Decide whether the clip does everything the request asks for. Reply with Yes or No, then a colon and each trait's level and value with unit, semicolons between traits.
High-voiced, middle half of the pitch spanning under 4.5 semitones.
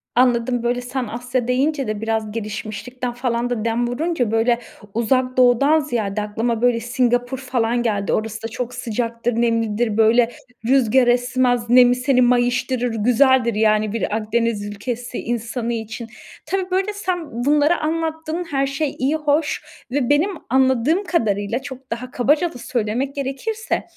Yes: high, 245 Hz; average, 2.7 semitones